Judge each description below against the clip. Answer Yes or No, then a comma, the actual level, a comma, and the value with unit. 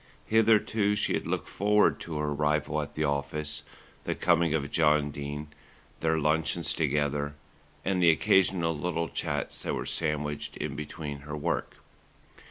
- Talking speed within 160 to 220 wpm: No, average, 150 wpm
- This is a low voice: Yes, very low, 75 Hz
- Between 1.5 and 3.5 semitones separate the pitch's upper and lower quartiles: Yes, narrow, 2.4 semitones